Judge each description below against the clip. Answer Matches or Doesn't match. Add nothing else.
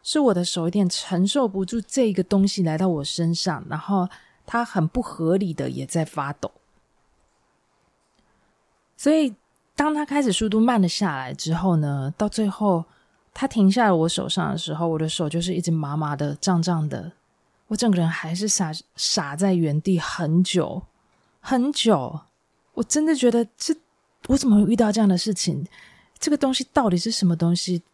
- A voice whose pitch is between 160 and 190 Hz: Matches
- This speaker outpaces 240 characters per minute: Matches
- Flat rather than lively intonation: Doesn't match